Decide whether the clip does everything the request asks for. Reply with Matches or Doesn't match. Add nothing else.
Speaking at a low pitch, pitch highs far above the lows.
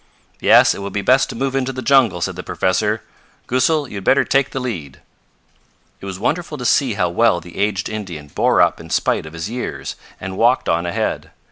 Matches